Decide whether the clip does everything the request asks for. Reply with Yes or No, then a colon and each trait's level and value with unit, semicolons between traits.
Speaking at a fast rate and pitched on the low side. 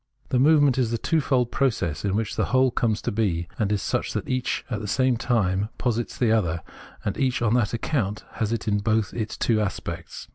Yes: fast, 220 wpm; low, 115 Hz